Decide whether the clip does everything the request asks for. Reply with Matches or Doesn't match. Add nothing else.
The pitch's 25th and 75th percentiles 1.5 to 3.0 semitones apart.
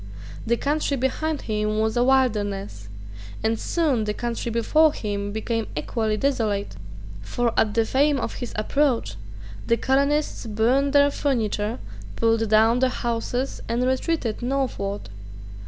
Doesn't match